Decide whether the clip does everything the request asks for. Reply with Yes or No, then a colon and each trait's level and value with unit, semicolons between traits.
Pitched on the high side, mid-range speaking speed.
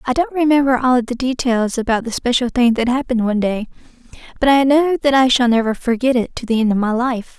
No: very high, 250 Hz; fast, 235 wpm